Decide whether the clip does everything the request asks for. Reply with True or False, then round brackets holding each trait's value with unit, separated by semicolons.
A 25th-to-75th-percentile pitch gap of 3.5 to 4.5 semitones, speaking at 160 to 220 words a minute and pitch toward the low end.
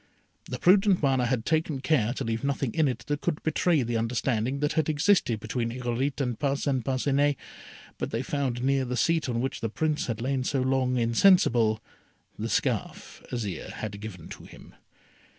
True (3.8 semitones; 180 wpm; 130 Hz)